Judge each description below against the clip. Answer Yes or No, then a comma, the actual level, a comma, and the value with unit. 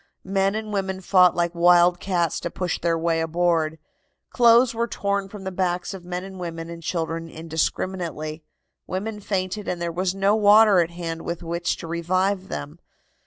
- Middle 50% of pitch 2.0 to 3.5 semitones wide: Yes, narrow, 2.6 semitones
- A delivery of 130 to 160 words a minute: No, average, 175 wpm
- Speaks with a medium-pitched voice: Yes, medium, 180 Hz